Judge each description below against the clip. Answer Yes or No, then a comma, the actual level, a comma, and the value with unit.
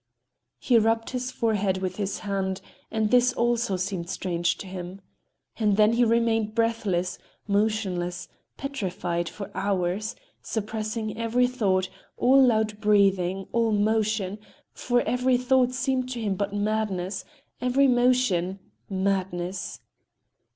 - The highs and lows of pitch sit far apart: No, average, 3.5 semitones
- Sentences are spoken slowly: Yes, slow, 115 wpm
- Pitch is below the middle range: No, high, 210 Hz